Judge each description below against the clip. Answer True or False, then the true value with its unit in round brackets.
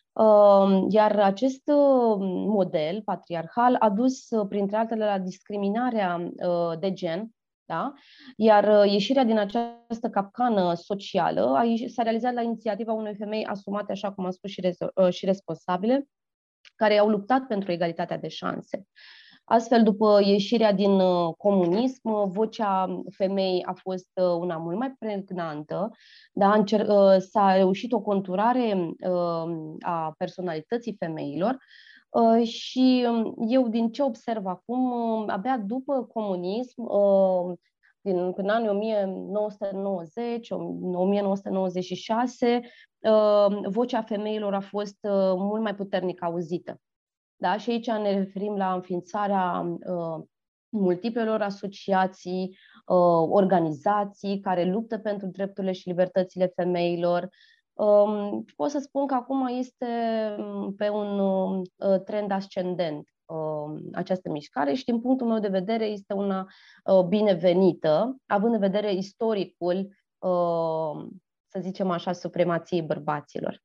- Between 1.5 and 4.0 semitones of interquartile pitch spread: True (3.4 semitones)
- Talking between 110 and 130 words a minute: True (115 wpm)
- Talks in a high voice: True (200 Hz)